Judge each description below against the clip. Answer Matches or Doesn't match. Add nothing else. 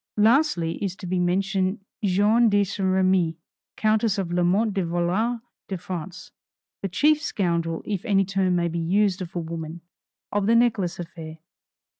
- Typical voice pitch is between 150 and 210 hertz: Matches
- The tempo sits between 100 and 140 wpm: Doesn't match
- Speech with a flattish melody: Doesn't match